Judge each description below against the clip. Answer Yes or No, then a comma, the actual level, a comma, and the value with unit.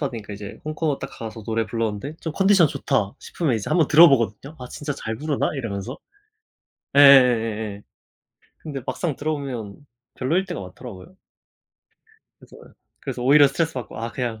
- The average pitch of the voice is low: Yes, low, 130 Hz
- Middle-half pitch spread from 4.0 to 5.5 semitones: Yes, average, 5.1 semitones